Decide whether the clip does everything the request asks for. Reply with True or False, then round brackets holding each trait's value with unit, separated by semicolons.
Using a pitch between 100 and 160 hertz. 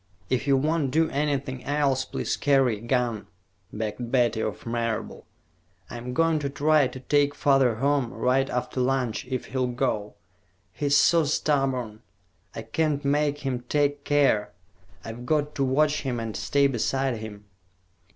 True (135 Hz)